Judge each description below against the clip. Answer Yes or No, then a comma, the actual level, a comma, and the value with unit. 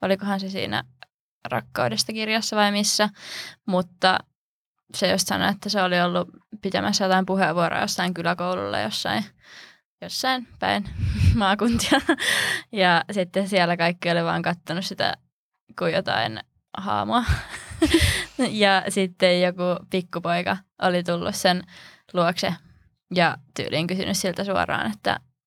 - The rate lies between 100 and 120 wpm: Yes, average, 115 wpm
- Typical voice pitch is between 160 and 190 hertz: Yes, medium, 185 Hz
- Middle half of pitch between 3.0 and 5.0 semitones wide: No, narrow, 2.5 semitones